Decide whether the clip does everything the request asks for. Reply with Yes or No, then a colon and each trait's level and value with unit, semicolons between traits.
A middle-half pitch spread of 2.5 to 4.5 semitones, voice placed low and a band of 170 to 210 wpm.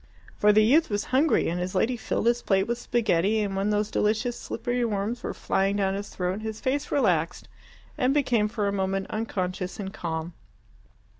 No: average, 3.7 semitones; high, 210 Hz; average, 190 wpm